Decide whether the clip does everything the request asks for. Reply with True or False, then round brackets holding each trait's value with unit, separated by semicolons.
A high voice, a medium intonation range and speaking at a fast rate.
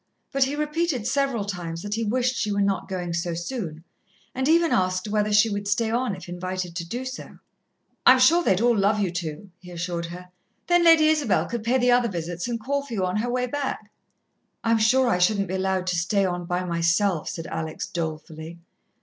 False (205 Hz; 5.8 semitones; 210 wpm)